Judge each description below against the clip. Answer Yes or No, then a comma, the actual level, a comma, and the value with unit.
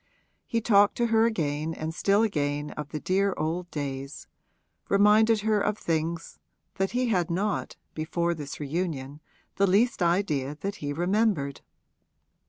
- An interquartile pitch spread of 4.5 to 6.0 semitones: Yes, wide, 5.5 semitones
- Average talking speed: Yes, average, 145 wpm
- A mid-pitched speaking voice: Yes, medium, 175 Hz